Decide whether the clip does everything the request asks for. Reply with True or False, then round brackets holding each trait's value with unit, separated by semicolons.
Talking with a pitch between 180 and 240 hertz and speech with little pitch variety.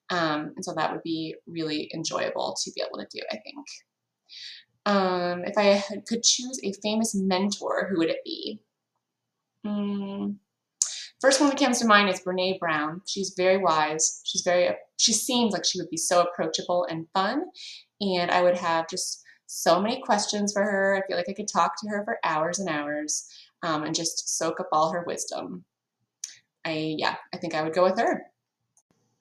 False (185 Hz; 3.8 semitones)